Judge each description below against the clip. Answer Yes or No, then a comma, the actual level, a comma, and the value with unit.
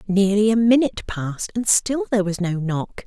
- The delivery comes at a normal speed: Yes, average, 195 wpm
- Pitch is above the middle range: Yes, high, 205 Hz